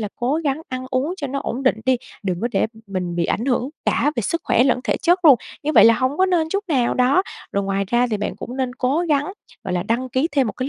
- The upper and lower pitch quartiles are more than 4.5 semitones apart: No, average, 4.1 semitones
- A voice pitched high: Yes, very high, 255 Hz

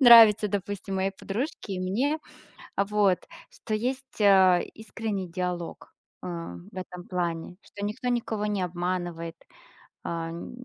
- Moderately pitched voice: No, high, 195 Hz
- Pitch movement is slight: No, average, 3.2 semitones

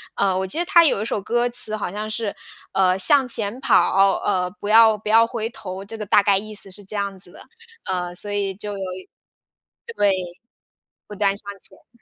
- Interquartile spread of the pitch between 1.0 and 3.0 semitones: Yes, narrow, 2.5 semitones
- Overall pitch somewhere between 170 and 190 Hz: No, high, 205 Hz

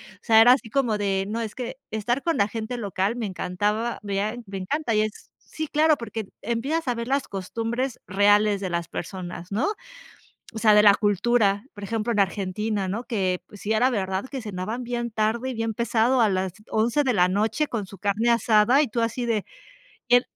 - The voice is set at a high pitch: Yes, high, 220 Hz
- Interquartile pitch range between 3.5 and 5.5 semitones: No, average, 3.0 semitones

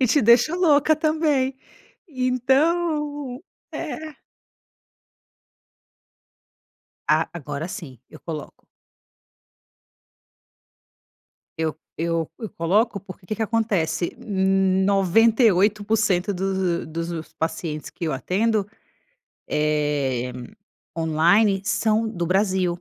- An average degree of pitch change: No, wide, 6.0 semitones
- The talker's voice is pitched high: Yes, high, 195 Hz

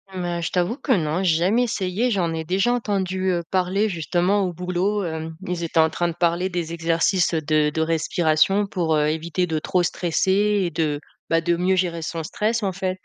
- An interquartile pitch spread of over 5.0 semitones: No, average, 2.7 semitones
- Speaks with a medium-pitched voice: Yes, medium, 175 Hz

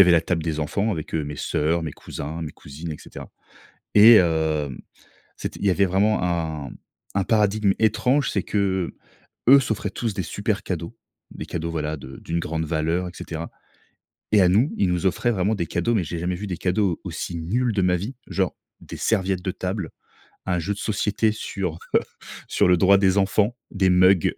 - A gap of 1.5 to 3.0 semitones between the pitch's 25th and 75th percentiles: No, average, 3.6 semitones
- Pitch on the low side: Yes, very low, 90 Hz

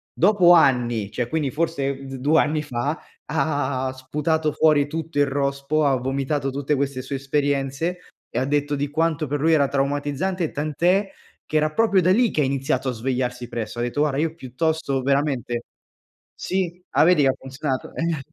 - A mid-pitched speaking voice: Yes, medium, 145 Hz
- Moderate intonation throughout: Yes, average, 3.0 semitones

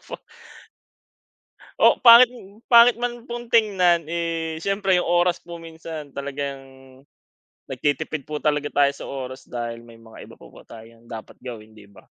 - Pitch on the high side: No, medium, 155 Hz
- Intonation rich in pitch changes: Yes, wide, 6.0 semitones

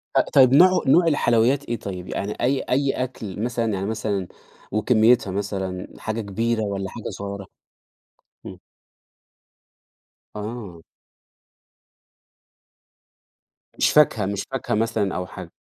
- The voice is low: Yes, low, 110 Hz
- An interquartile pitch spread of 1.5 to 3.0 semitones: No, average, 3.7 semitones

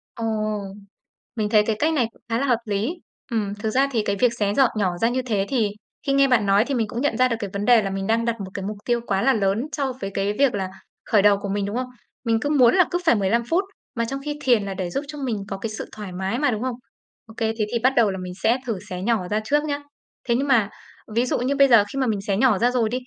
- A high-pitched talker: Yes, high, 225 Hz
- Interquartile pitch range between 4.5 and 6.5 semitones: No, average, 4.0 semitones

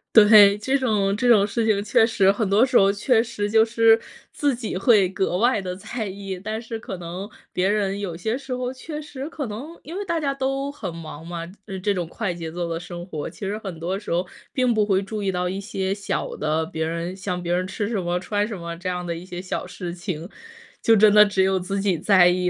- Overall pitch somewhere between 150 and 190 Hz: No, high, 200 Hz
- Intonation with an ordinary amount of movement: Yes, average, 3.8 semitones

